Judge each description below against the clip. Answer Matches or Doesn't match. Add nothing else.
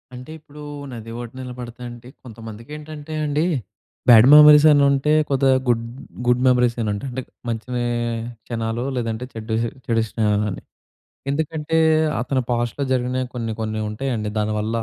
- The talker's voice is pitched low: Matches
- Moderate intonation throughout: Matches